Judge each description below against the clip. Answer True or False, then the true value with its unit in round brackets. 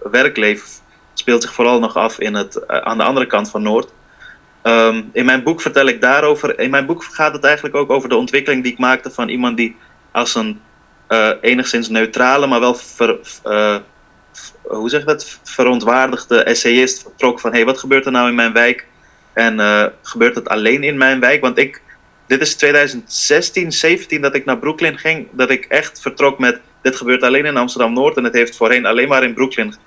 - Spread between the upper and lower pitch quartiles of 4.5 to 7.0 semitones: False (2.9 semitones)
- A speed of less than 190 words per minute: False (200 wpm)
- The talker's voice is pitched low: True (125 Hz)